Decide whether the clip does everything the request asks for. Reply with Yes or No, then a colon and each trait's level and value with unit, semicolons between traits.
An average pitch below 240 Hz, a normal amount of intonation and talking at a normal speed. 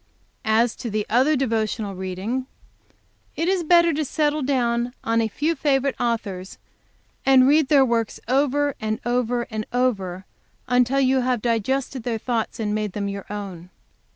No: high, 245 Hz; average, 3.9 semitones; average, 155 wpm